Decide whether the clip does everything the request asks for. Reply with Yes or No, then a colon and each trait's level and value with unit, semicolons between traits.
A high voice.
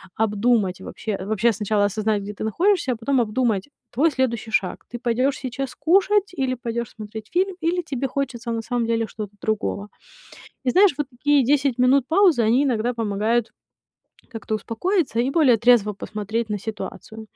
Yes: high, 235 Hz